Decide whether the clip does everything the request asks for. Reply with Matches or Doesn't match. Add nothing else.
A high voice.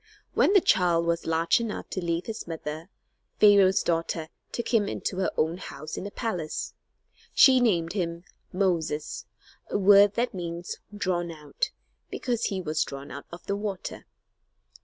Doesn't match